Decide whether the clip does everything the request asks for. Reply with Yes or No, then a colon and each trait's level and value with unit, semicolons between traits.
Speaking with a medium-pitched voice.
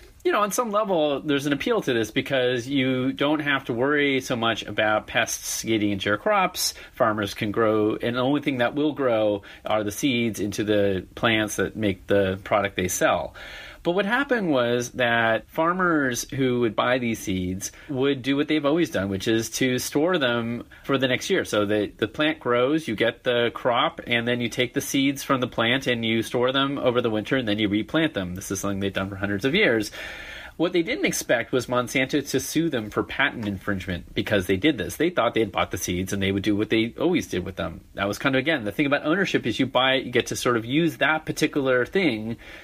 No: low, 120 Hz